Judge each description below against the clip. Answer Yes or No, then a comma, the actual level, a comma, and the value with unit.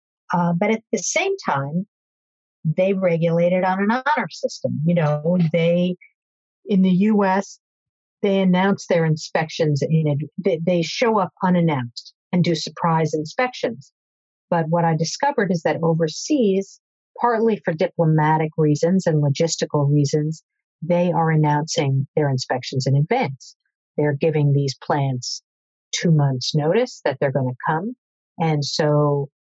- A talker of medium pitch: Yes, medium, 165 Hz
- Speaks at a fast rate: No, average, 140 wpm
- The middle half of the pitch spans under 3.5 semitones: No, average, 3.9 semitones